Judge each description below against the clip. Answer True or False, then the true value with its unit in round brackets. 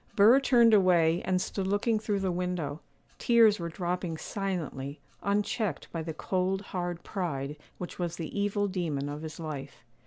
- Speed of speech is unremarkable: True (160 wpm)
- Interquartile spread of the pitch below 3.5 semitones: False (3.9 semitones)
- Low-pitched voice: False (180 Hz)